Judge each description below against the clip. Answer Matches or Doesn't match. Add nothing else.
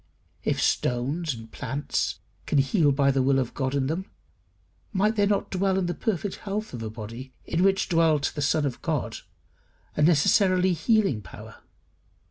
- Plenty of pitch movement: Matches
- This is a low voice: Doesn't match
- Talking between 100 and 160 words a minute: Doesn't match